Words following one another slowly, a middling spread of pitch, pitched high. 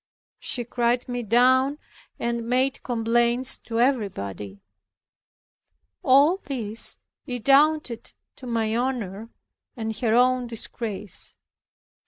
No: slow, 95 wpm; narrow, 2.3 semitones; high, 240 Hz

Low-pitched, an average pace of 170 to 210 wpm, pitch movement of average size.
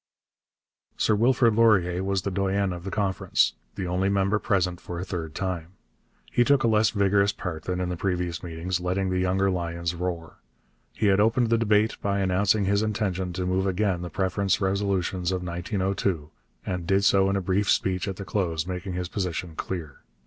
No: very low, 95 Hz; average, 190 wpm; narrow, 1.9 semitones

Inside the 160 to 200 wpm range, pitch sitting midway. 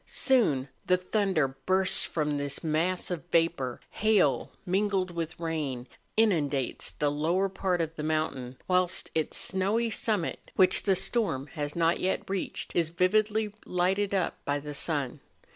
No: average, 145 wpm; medium, 170 Hz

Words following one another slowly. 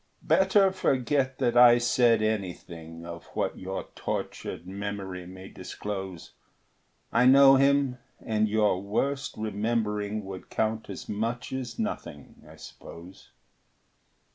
Yes: slow, 115 wpm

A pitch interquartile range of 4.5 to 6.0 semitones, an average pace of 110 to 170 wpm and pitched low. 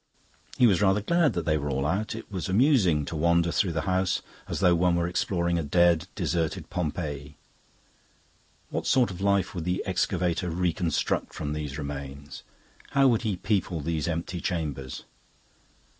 No: average, 3.6 semitones; average, 165 wpm; very low, 85 Hz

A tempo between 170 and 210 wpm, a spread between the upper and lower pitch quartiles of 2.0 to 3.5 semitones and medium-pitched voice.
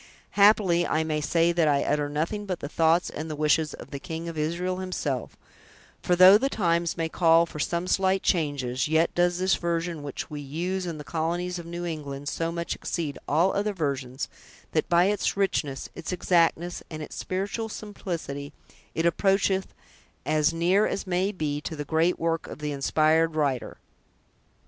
Yes: average, 180 wpm; average, 2.9 semitones; medium, 165 Hz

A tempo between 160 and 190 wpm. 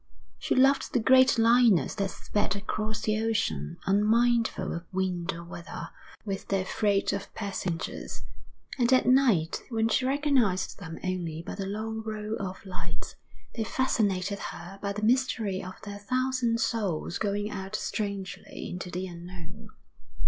No: average, 150 wpm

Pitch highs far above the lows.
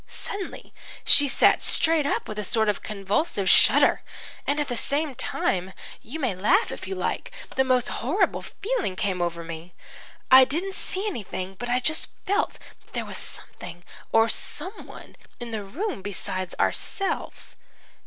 Yes: wide, 8.5 semitones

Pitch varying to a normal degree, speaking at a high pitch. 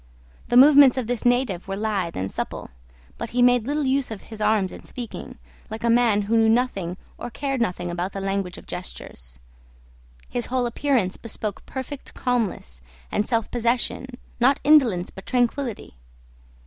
Yes: average, 4.3 semitones; high, 230 Hz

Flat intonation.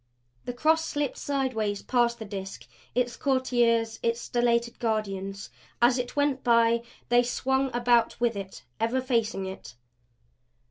Yes: narrow, 2.2 semitones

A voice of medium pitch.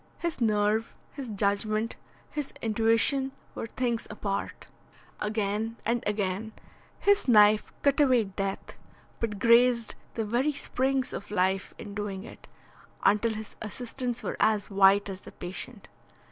No: high, 220 Hz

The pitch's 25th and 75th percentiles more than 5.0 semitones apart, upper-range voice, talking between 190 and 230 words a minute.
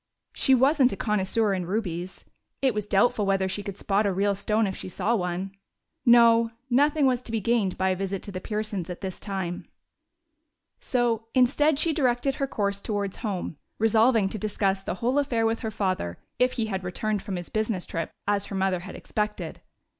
No: average, 3.5 semitones; high, 210 Hz; average, 195 wpm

